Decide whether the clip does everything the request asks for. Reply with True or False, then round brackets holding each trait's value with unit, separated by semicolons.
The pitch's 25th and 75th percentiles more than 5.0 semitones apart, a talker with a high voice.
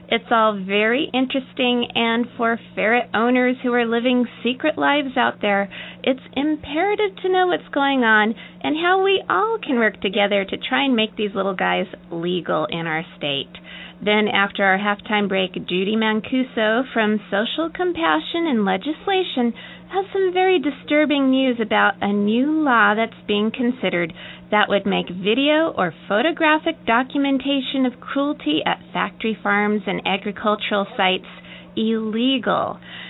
True (5.4 semitones; 230 Hz)